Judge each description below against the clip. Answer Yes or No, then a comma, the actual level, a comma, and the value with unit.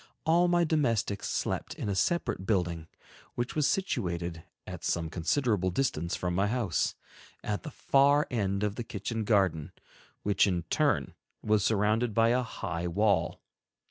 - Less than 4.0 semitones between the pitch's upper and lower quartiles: No, wide, 5.4 semitones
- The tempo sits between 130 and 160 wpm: Yes, average, 150 wpm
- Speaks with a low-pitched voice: Yes, low, 105 Hz